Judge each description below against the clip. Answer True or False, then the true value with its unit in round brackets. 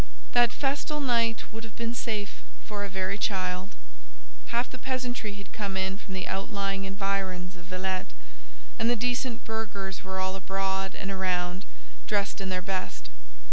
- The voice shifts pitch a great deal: False (3.0 semitones)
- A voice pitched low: False (195 Hz)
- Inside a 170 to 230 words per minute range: False (160 wpm)